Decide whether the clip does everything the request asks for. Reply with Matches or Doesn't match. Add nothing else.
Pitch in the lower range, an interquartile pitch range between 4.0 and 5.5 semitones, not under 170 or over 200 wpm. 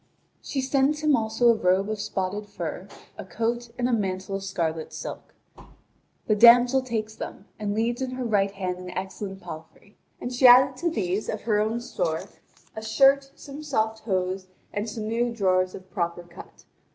Doesn't match